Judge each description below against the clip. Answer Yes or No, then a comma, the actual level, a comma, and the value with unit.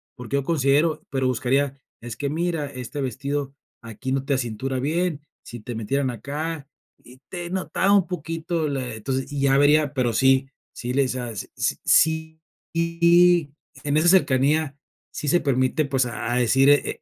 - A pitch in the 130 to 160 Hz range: Yes, medium, 140 Hz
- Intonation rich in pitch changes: No, average, 3.6 semitones